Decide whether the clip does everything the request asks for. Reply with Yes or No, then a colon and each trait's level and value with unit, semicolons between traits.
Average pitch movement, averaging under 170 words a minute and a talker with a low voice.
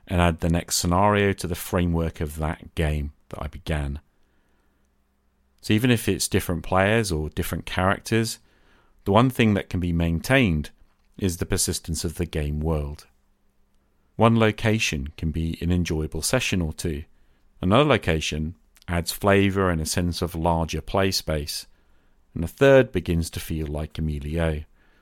Yes: average, 3.8 semitones; average, 160 wpm; very low, 85 Hz